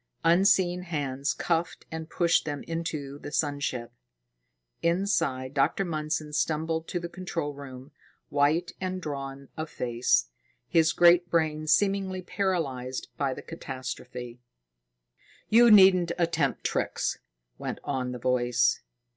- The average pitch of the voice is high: No, medium, 155 Hz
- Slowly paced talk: Yes, slow, 120 wpm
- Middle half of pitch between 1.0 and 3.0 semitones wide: No, average, 4.2 semitones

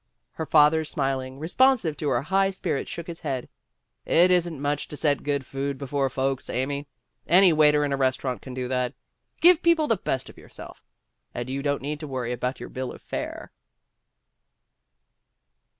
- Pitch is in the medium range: Yes, medium, 145 Hz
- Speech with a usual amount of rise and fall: Yes, average, 3.6 semitones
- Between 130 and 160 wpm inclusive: No, average, 175 wpm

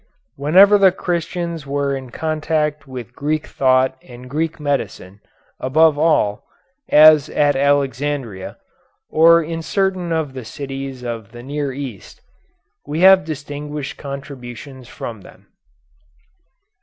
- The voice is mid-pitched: Yes, medium, 145 Hz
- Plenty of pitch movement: No, average, 3.2 semitones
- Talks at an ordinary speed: No, slow, 120 wpm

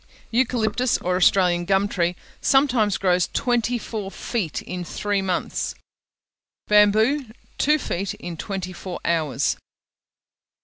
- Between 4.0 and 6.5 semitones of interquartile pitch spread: Yes, average, 4.4 semitones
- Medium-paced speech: No, slow, 115 wpm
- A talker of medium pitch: No, high, 200 Hz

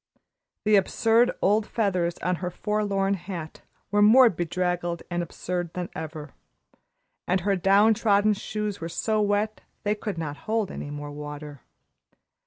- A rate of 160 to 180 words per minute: No, average, 145 wpm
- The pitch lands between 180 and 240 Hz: Yes, high, 190 Hz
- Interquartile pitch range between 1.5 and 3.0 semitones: No, average, 3.6 semitones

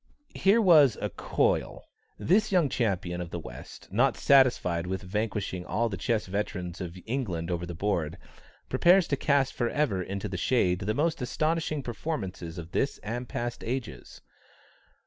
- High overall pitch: No, low, 110 Hz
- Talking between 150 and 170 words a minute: Yes, average, 160 wpm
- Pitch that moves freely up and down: Yes, wide, 7.5 semitones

